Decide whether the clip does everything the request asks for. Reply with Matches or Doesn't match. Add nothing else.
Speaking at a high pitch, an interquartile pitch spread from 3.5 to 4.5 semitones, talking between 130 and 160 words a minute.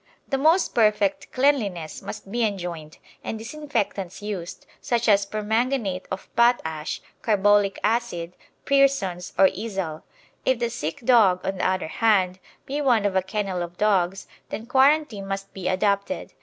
Matches